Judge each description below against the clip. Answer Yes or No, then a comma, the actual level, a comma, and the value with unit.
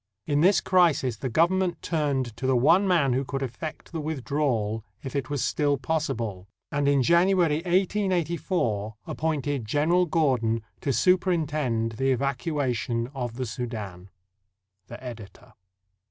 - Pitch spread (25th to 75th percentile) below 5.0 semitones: No, wide, 5.5 semitones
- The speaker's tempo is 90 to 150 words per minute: Yes, average, 140 wpm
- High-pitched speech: No, medium, 140 Hz